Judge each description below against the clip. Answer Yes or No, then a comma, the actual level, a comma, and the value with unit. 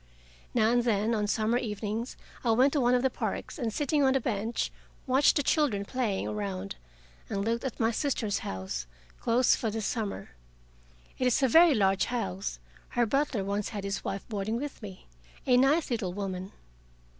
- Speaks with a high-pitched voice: Yes, high, 225 Hz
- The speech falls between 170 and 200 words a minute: Yes, average, 180 wpm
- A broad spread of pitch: No, average, 4.2 semitones